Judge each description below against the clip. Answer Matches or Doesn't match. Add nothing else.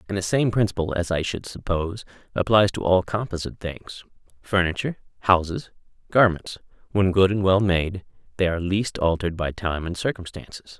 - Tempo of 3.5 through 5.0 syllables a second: Doesn't match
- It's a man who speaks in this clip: Matches